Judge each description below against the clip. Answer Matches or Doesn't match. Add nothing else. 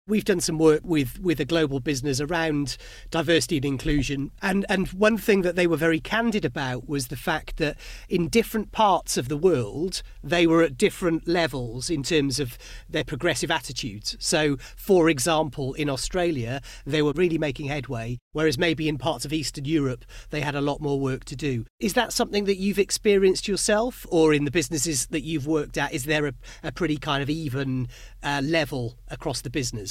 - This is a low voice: Doesn't match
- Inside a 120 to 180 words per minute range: Doesn't match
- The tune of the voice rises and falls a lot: Doesn't match